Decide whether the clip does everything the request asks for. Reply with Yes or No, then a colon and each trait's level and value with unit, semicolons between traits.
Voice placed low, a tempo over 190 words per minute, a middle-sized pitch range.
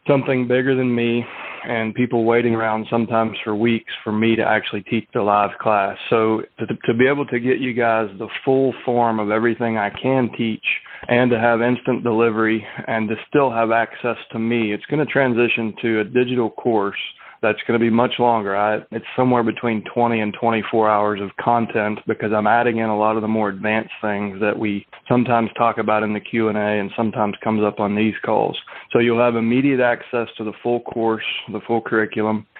No: low, 115 Hz; average, 200 wpm; narrow, 1.8 semitones